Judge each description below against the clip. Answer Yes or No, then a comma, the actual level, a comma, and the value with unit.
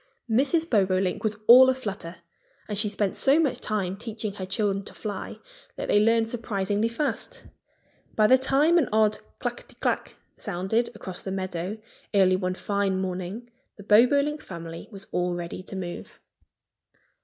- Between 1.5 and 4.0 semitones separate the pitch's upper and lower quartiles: Yes, average, 3.7 semitones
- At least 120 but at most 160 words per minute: Yes, average, 155 wpm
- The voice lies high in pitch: Yes, high, 205 Hz